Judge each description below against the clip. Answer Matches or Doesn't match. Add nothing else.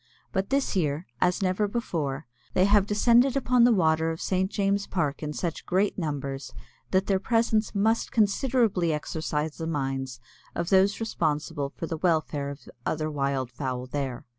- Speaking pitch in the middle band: Matches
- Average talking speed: Matches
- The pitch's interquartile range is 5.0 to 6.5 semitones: Matches